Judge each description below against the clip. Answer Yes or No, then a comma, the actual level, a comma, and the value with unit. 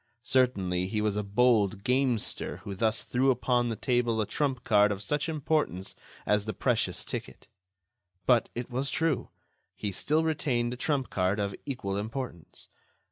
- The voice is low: Yes, low, 120 Hz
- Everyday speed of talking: Yes, average, 160 wpm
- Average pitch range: Yes, average, 4.3 semitones